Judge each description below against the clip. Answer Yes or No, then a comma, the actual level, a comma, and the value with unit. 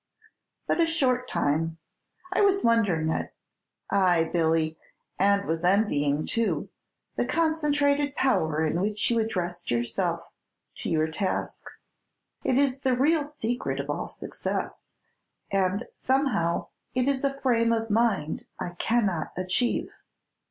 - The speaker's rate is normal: No, slow, 130 wpm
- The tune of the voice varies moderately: No, wide, 8.1 semitones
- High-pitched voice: Yes, high, 210 Hz